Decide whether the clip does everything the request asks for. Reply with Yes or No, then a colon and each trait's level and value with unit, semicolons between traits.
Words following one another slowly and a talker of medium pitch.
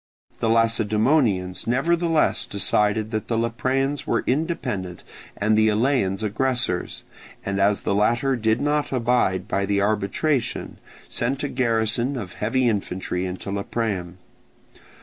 No: slow, 125 wpm; low, 110 Hz